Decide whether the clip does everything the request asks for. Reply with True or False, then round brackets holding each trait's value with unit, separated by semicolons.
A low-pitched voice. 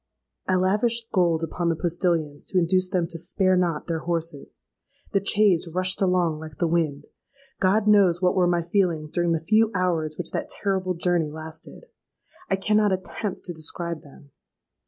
False (175 Hz)